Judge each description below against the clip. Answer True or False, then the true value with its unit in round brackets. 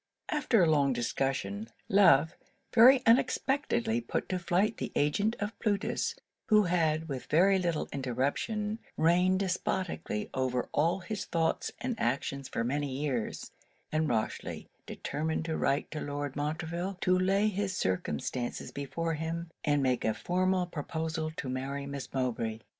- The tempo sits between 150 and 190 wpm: False (140 wpm)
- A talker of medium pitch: True (160 Hz)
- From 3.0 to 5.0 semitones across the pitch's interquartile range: False (5.6 semitones)